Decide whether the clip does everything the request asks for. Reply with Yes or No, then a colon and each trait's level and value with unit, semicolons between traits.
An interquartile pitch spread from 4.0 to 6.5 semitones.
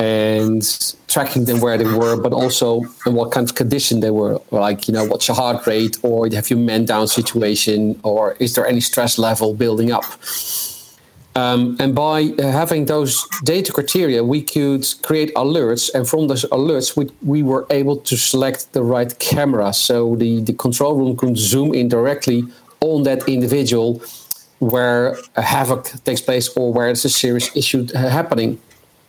No: average, 3.3 semitones